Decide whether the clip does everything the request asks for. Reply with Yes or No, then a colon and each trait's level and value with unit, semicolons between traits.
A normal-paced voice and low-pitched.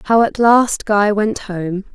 No: average, 185 wpm; high, 210 Hz